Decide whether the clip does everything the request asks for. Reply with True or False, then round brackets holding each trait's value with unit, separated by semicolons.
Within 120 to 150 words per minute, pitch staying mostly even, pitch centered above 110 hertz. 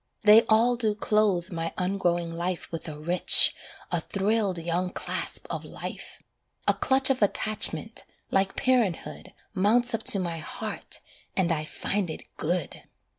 False (145 wpm; 4.1 semitones; 190 Hz)